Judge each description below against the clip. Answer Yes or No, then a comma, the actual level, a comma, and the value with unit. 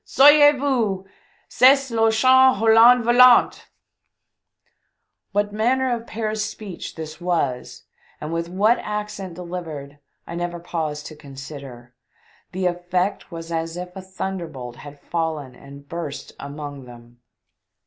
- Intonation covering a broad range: Yes, wide, 6.8 semitones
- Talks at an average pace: No, slow, 130 wpm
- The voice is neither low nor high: Yes, medium, 175 Hz